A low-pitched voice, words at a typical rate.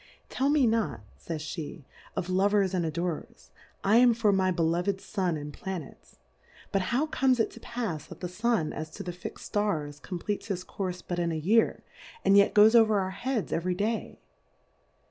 No: high, 190 Hz; average, 185 wpm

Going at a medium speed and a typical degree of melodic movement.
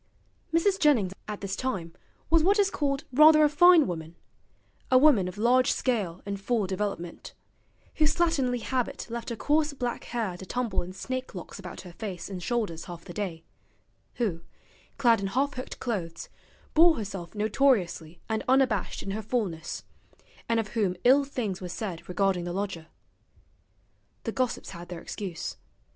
No: average, 165 wpm; wide, 6.1 semitones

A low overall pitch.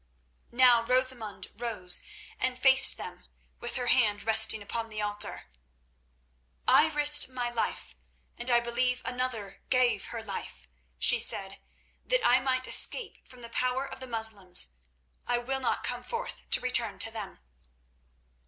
No: high, 240 Hz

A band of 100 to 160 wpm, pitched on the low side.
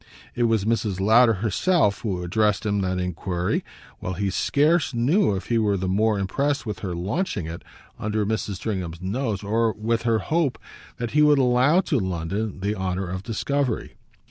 No: average, 175 wpm; low, 105 Hz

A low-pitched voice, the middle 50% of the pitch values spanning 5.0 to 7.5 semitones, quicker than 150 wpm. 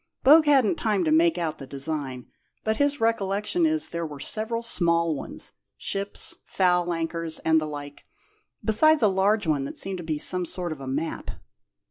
No: medium, 175 Hz; wide, 5.6 semitones; average, 180 wpm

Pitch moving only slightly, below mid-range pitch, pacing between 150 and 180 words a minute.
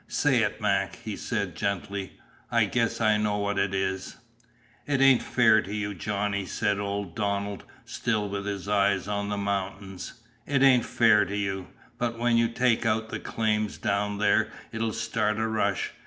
Yes: narrow, 1.9 semitones; low, 105 Hz; average, 175 wpm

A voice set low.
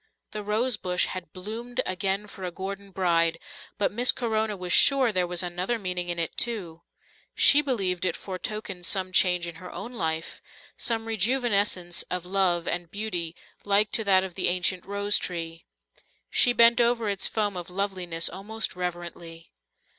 No: high, 190 Hz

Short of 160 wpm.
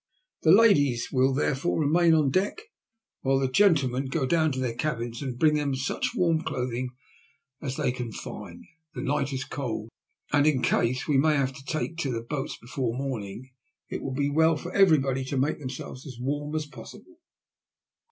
No: average, 180 wpm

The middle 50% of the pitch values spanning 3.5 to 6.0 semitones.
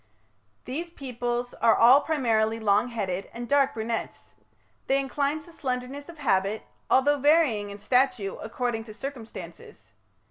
Yes: average, 4.0 semitones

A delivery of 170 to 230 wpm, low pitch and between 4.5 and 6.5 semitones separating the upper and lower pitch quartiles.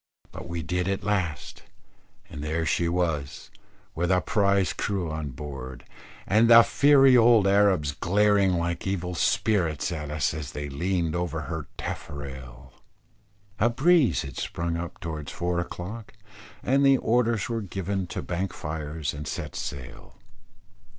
No: average, 145 wpm; very low, 85 Hz; average, 5.0 semitones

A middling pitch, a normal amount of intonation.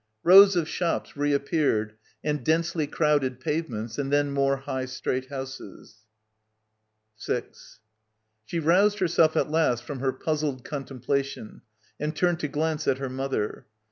Yes: medium, 145 Hz; average, 3.5 semitones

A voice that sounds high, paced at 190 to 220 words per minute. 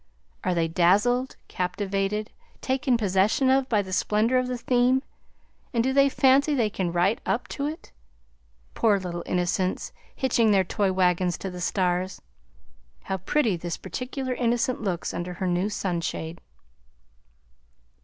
No: high, 205 Hz; average, 145 wpm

